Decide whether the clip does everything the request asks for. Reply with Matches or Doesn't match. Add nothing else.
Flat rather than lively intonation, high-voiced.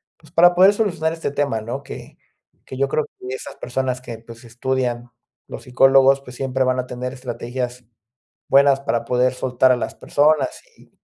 Doesn't match